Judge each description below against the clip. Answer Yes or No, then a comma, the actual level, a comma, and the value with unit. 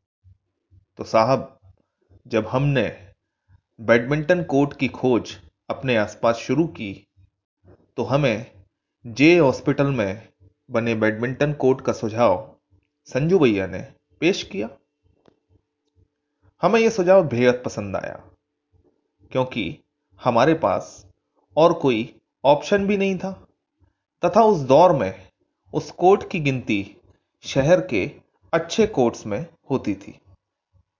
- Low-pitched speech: Yes, low, 120 Hz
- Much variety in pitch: Yes, wide, 6.8 semitones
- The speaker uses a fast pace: No, slow, 110 wpm